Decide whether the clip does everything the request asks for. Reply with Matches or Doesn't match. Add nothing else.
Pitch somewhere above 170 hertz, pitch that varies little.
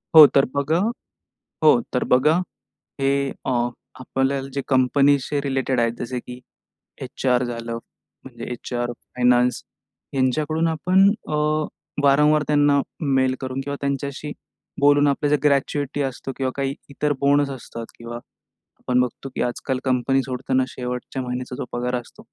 Doesn't match